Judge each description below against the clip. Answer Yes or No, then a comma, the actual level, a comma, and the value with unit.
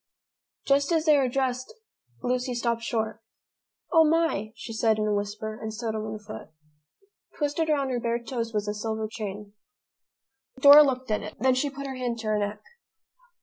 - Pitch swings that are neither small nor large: Yes, average, 4.0 semitones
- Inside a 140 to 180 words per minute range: No, average, 190 wpm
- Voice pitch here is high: Yes, high, 235 Hz